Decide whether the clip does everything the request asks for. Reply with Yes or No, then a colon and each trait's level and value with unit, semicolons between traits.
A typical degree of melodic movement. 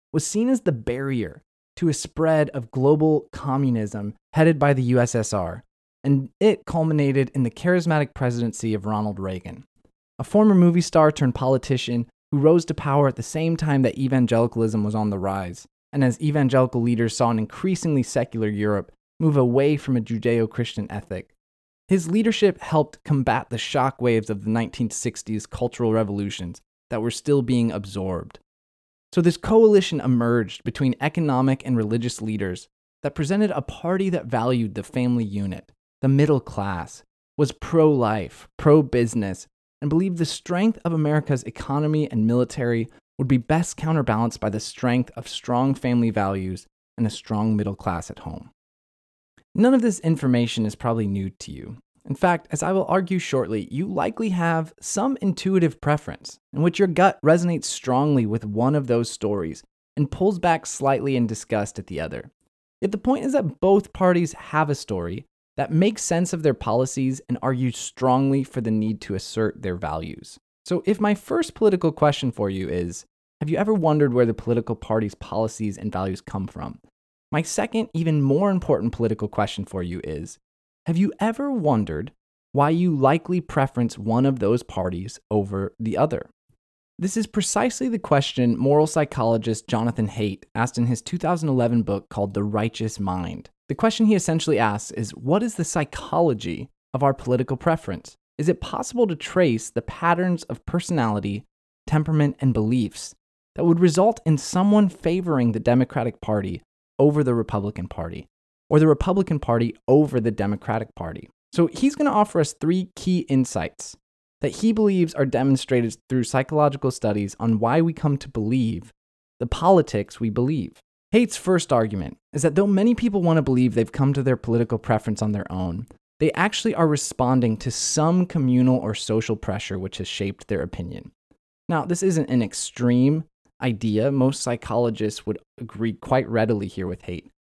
No: wide, 6.4 semitones